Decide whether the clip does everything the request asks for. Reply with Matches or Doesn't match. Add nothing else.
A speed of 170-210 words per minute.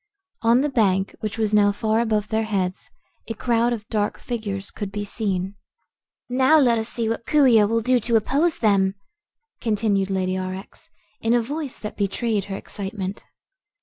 Matches